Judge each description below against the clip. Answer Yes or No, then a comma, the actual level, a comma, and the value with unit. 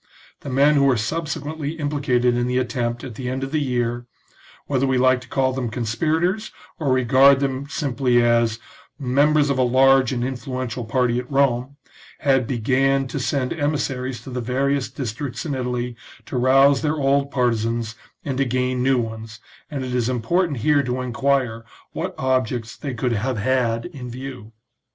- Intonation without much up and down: Yes, narrow, 2.3 semitones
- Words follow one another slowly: No, average, 175 wpm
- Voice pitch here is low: Yes, low, 130 Hz